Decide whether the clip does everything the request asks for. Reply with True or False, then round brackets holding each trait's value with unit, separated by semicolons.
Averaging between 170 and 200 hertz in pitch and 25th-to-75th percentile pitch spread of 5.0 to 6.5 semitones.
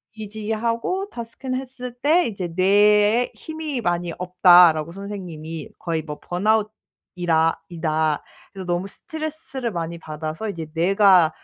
True (195 Hz; 5.4 semitones)